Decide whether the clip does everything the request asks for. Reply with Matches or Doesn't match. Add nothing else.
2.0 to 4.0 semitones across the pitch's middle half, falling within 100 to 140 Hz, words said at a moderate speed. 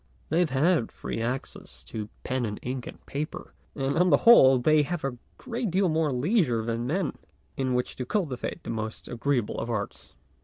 Doesn't match